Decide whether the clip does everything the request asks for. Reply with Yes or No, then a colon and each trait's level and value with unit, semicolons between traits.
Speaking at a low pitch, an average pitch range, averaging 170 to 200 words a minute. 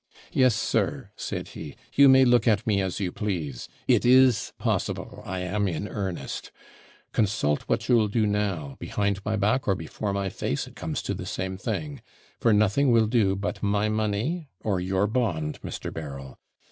Yes: low, 105 Hz; average, 3.3 semitones; average, 175 wpm